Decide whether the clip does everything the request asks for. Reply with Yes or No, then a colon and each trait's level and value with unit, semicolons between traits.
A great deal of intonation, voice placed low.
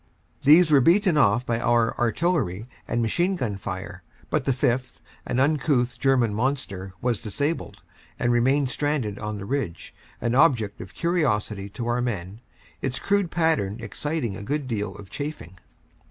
Yes: wide, 5.9 semitones; low, 120 Hz